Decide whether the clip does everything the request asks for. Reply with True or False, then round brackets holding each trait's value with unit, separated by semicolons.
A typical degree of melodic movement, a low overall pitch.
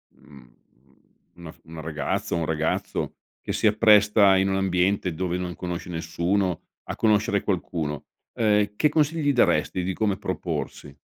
True (3.8 semitones; 95 Hz)